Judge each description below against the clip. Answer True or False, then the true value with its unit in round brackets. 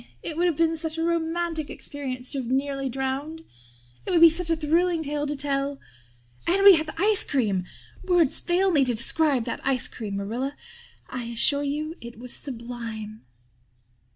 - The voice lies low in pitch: False (285 Hz)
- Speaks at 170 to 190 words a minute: True (180 wpm)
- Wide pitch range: False (4.5 semitones)